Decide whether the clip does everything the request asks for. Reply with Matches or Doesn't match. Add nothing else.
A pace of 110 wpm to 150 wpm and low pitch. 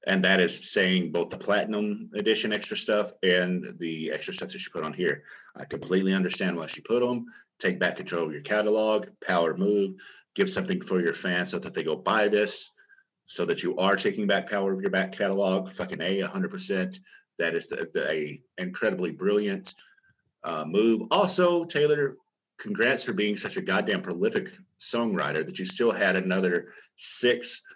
Doesn't match